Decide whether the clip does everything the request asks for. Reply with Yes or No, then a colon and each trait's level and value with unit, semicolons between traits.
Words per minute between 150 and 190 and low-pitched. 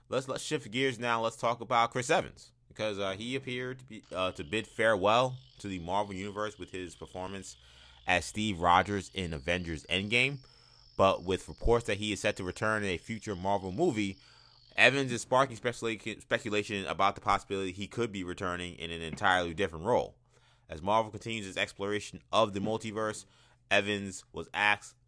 Yes: average, 180 wpm; low, 105 Hz